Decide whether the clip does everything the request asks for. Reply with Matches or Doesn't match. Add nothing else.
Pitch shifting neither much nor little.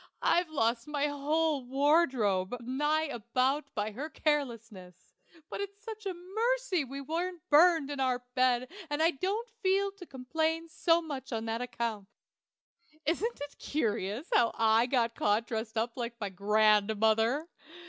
Doesn't match